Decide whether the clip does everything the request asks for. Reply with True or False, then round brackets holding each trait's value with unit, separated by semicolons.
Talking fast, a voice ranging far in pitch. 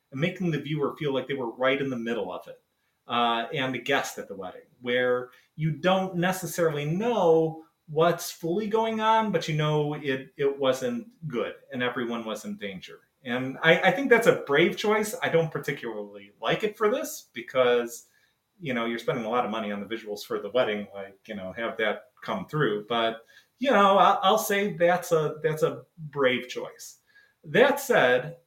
False (195 wpm; 7.0 semitones)